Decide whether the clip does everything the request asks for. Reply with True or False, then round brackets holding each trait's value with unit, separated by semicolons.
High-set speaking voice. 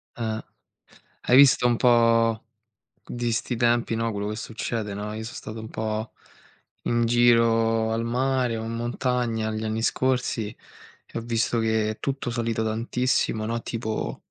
False (115 Hz)